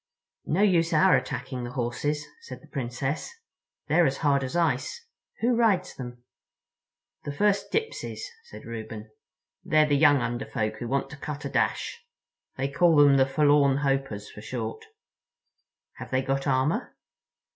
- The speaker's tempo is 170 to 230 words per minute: No, average, 155 wpm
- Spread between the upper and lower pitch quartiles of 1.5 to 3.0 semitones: No, average, 3.9 semitones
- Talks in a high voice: No, medium, 140 Hz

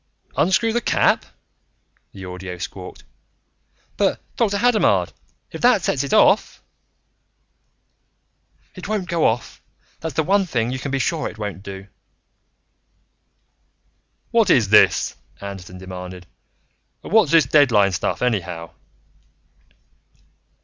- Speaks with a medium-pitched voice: No, low, 125 Hz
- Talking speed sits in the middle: No, slow, 120 wpm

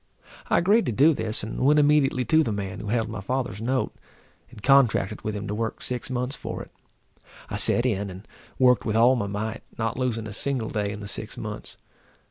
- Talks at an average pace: No, fast, 215 wpm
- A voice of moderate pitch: No, low, 115 Hz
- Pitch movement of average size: Yes, average, 3.7 semitones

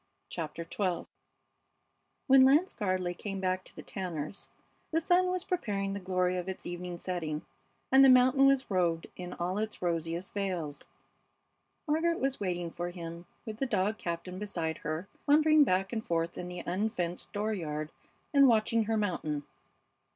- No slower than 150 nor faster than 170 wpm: Yes, average, 160 wpm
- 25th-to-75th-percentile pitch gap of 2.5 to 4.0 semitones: No, average, 4.7 semitones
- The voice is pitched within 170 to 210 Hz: Yes, medium, 185 Hz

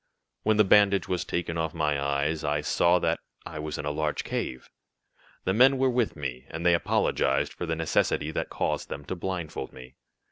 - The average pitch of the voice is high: No, very low, 80 Hz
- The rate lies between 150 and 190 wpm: No, average, 200 wpm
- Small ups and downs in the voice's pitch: No, average, 4.1 semitones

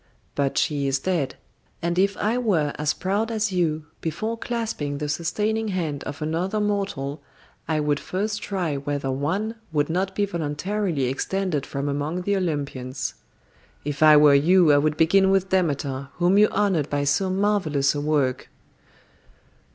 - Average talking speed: Yes, average, 160 wpm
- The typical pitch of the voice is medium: Yes, medium, 160 Hz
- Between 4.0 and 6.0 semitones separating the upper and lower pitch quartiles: Yes, average, 5.2 semitones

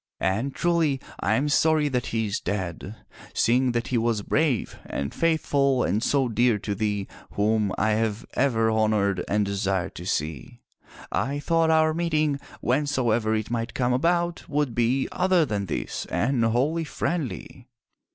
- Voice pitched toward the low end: Yes, low, 120 Hz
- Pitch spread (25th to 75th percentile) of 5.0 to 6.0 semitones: Yes, wide, 5.6 semitones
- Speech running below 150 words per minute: No, average, 155 wpm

